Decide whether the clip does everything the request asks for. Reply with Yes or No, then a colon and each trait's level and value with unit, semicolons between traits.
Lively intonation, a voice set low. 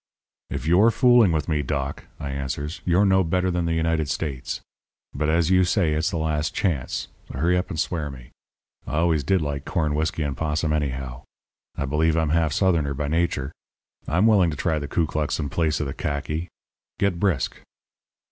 No: average, 3.0 semitones; very low, 80 Hz